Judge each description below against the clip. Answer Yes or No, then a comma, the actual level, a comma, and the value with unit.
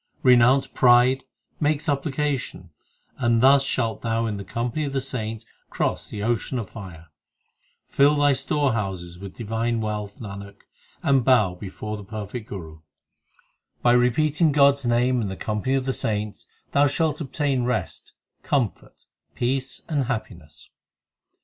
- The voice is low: Yes, low, 120 Hz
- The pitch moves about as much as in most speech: Yes, average, 4.4 semitones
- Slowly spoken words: No, average, 145 wpm